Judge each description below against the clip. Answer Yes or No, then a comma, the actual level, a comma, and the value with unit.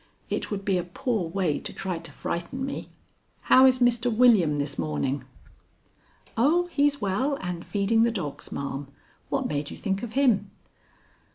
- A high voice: Yes, high, 200 Hz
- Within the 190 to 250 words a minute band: No, average, 165 wpm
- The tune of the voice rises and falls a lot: Yes, wide, 6.7 semitones